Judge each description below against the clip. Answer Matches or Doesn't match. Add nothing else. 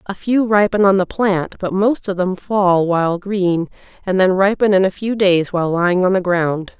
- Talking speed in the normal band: Doesn't match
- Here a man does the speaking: Doesn't match